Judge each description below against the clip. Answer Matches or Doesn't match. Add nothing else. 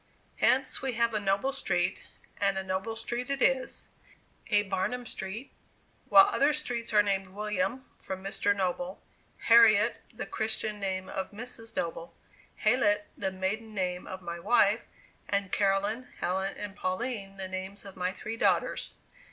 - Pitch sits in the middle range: Doesn't match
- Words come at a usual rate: Matches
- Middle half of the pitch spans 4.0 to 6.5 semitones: Doesn't match